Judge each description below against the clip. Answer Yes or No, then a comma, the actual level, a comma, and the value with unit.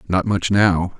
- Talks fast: No, average, 180 wpm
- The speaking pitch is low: Yes, very low, 90 Hz